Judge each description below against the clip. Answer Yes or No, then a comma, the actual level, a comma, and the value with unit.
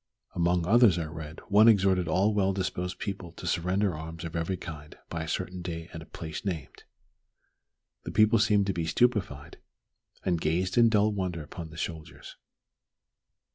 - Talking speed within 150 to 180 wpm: Yes, average, 170 wpm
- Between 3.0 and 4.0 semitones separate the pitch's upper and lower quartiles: Yes, average, 3.3 semitones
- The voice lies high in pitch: No, very low, 90 Hz